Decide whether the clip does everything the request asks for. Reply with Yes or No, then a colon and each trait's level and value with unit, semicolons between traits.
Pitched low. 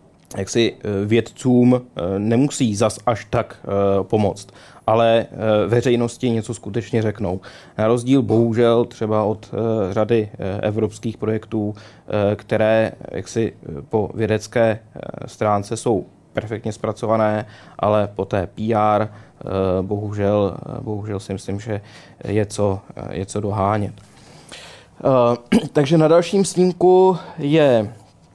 Yes: low, 110 Hz